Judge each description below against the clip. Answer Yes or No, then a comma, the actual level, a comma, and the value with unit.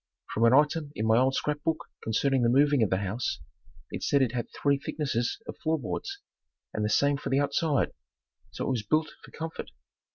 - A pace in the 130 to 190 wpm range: No, fast, 205 wpm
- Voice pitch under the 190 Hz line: Yes, medium, 140 Hz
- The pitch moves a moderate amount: Yes, average, 4.1 semitones